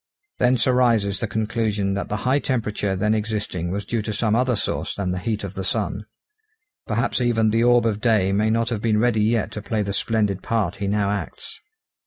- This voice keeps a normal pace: No, fast, 210 wpm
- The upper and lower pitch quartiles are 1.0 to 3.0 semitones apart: Yes, narrow, 2.4 semitones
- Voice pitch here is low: Yes, low, 110 Hz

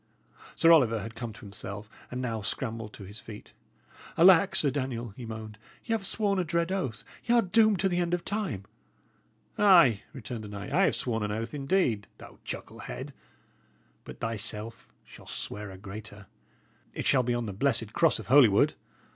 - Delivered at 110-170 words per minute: No, average, 180 wpm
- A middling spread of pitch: No, wide, 8.0 semitones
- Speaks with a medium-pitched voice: No, low, 120 Hz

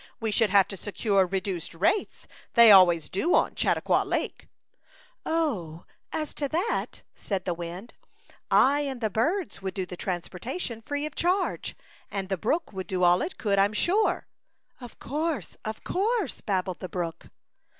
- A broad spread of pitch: Yes, wide, 8.0 semitones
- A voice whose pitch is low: No, high, 210 Hz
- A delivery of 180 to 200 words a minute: No, average, 170 wpm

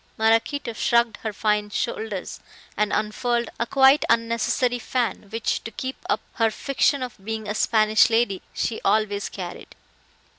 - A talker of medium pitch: No, high, 225 Hz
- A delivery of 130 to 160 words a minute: Yes, average, 145 wpm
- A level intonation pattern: Yes, narrow, 2.1 semitones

